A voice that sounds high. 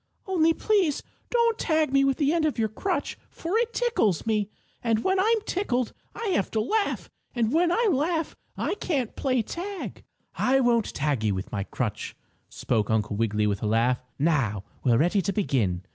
Yes: high, 240 Hz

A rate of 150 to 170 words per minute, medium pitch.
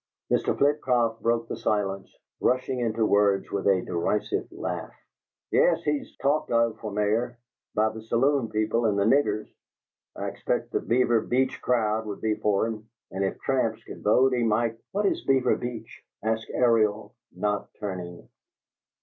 No: average, 160 wpm; low, 110 Hz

